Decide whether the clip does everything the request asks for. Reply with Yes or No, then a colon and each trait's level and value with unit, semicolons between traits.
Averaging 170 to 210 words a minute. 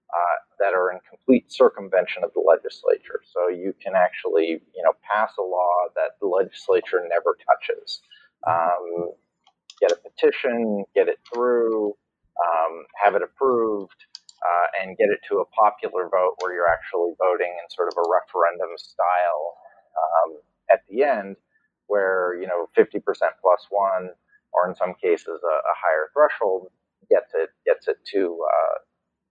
No: average, 155 wpm